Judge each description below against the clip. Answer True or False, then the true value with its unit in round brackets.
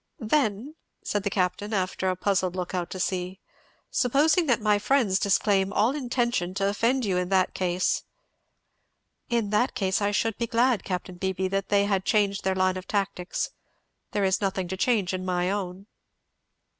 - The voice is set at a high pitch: True (195 Hz)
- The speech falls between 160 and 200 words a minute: True (180 wpm)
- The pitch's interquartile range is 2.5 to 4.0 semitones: True (2.9 semitones)